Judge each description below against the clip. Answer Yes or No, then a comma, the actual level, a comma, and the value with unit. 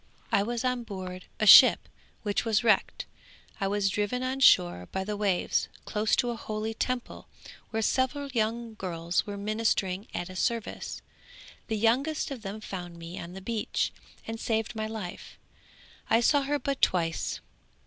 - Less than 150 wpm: No, average, 165 wpm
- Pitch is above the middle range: Yes, high, 215 Hz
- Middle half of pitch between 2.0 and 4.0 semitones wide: Yes, average, 3.6 semitones